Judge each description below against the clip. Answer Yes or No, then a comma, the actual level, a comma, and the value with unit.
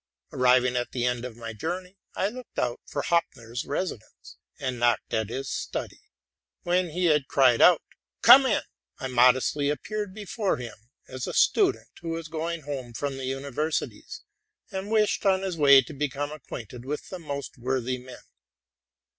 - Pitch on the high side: No, medium, 140 Hz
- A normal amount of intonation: No, wide, 5.7 semitones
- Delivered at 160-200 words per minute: Yes, average, 170 wpm